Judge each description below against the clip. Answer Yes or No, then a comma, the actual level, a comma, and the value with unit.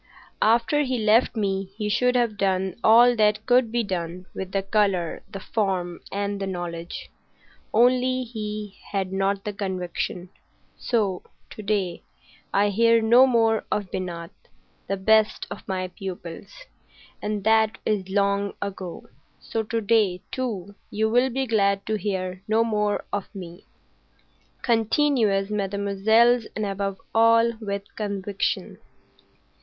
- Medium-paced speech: No, slow, 130 wpm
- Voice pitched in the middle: No, high, 205 Hz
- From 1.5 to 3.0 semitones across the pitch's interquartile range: Yes, average, 2.7 semitones